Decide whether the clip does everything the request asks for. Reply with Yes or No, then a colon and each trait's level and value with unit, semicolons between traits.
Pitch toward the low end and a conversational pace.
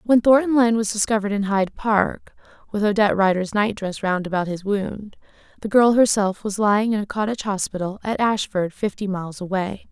No: high, 205 Hz; average, 190 wpm